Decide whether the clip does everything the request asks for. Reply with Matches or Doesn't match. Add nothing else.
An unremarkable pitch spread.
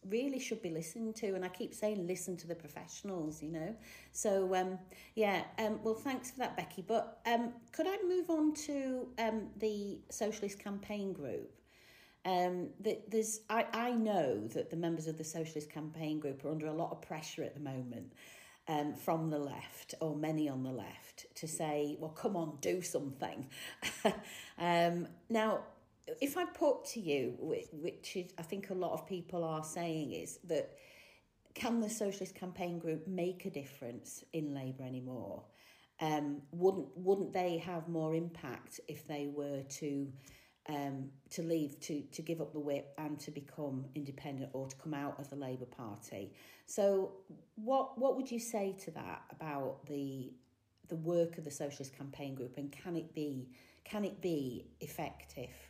Doesn't match